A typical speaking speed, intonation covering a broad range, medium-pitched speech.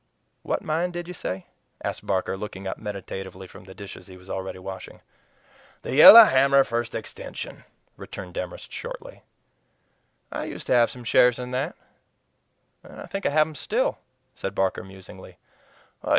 No: average, 160 wpm; wide, 6.4 semitones; low, 105 Hz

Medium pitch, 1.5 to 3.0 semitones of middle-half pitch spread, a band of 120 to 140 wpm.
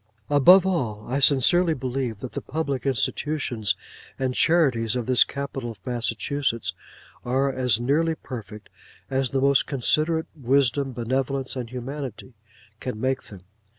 No: low, 130 Hz; average, 2.7 semitones; slow, 135 wpm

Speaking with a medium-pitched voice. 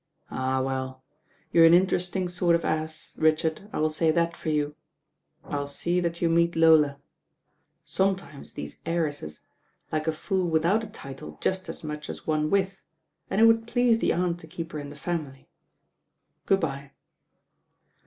Yes: medium, 165 Hz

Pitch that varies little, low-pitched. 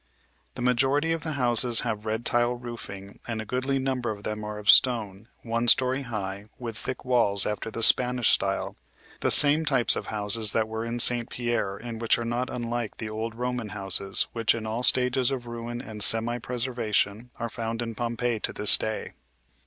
Yes: narrow, 2.3 semitones; low, 115 Hz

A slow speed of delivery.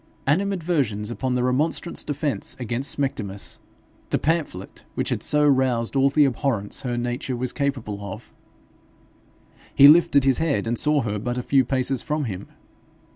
No: average, 155 wpm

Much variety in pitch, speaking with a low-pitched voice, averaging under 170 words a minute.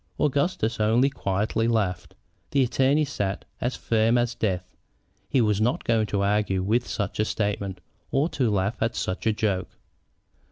No: average, 3.4 semitones; low, 110 Hz; average, 160 wpm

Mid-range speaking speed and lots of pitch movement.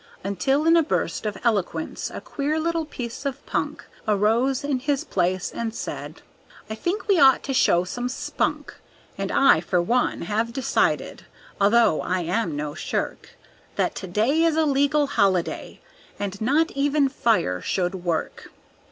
Yes: average, 160 wpm; wide, 6.7 semitones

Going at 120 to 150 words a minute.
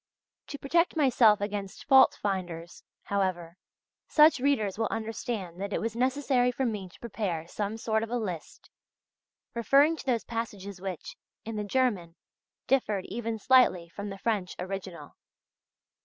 Yes: average, 145 wpm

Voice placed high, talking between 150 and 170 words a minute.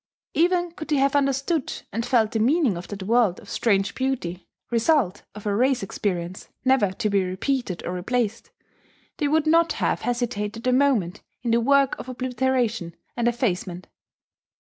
Yes: high, 240 Hz; average, 165 wpm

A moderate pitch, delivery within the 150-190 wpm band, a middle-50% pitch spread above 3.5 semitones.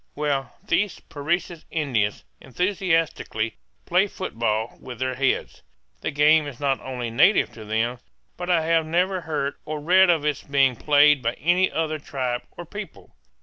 Yes: medium, 145 Hz; average, 155 wpm; average, 4.8 semitones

